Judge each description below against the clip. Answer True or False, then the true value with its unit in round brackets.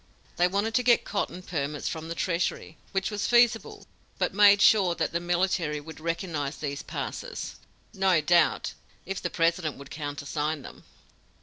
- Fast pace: False (160 wpm)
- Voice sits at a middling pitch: True (175 Hz)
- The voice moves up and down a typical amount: True (4.2 semitones)